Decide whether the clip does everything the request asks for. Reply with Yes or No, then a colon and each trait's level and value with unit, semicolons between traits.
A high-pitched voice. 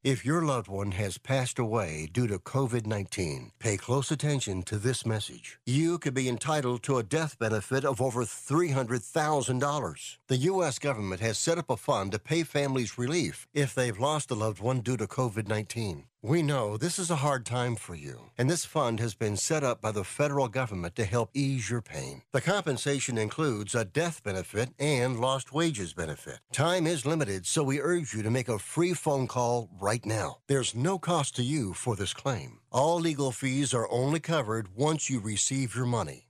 No: low, 130 Hz